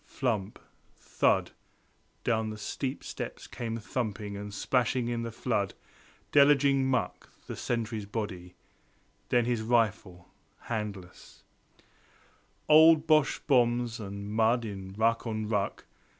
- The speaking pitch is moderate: No, low, 115 Hz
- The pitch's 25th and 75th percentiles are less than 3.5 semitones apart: Yes, average, 3.0 semitones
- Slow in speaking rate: Yes, slow, 120 wpm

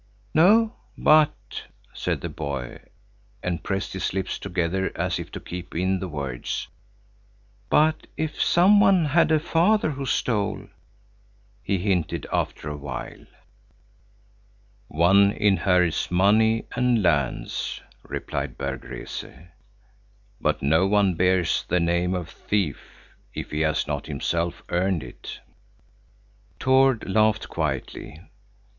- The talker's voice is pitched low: Yes, very low, 95 Hz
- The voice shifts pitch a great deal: Yes, wide, 6.7 semitones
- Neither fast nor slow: No, slow, 120 wpm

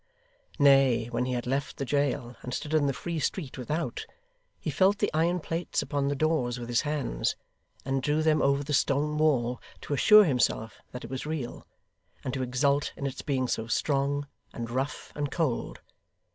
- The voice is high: No, medium, 140 Hz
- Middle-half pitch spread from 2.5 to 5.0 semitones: Yes, average, 3.3 semitones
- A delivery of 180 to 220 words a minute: Yes, average, 185 wpm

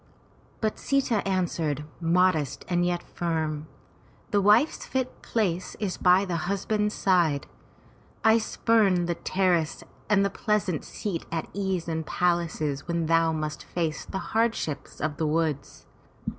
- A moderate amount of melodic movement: Yes, average, 3.7 semitones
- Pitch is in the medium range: Yes, medium, 175 Hz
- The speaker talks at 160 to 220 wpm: No, slow, 135 wpm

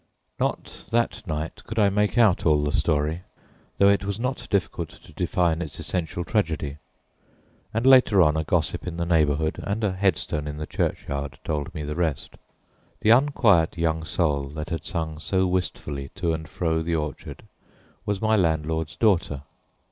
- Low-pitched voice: Yes, very low, 85 Hz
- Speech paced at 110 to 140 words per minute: No, average, 170 wpm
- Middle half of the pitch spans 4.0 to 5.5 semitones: Yes, average, 4.5 semitones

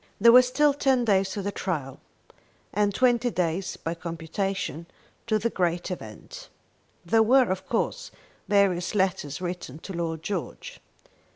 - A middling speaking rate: Yes, average, 145 wpm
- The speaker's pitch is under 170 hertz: No, high, 190 Hz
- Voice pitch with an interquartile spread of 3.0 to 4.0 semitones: No, average, 5.0 semitones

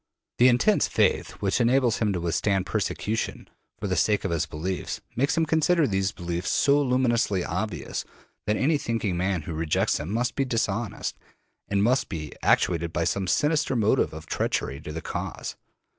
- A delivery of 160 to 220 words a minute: Yes, average, 175 wpm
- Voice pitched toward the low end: Yes, low, 105 Hz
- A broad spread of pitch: Yes, wide, 6.2 semitones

